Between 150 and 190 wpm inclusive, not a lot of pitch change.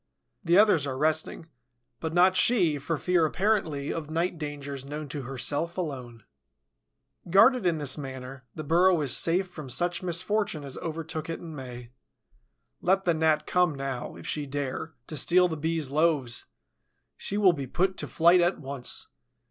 No: average, 170 wpm; average, 4.0 semitones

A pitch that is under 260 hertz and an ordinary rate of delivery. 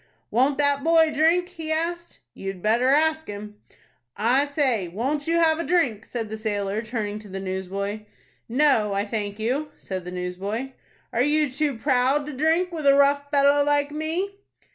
No: very high, 270 Hz; average, 180 wpm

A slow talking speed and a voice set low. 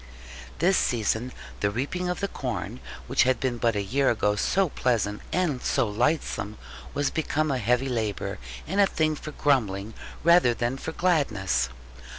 No: average, 160 wpm; low, 125 Hz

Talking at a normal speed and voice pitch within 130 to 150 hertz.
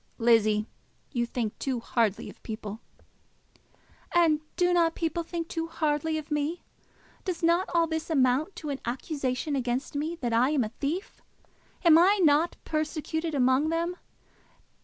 No: average, 150 wpm; very high, 305 Hz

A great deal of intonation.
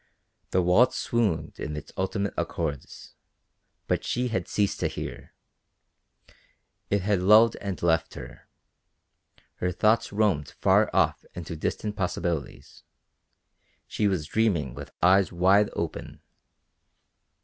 No: average, 3.6 semitones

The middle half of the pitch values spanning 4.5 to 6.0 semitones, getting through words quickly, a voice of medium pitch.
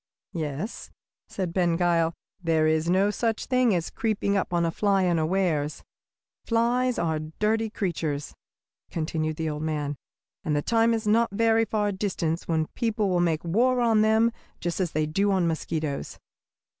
No: wide, 5.4 semitones; average, 160 wpm; medium, 180 Hz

